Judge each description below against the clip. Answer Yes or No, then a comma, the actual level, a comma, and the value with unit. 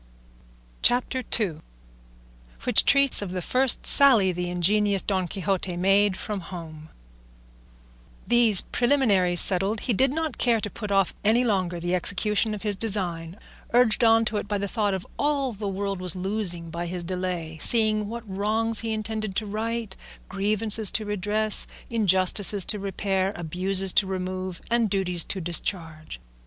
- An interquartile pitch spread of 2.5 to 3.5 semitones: Yes, average, 3.1 semitones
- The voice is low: No, high, 200 Hz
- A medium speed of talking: Yes, average, 155 wpm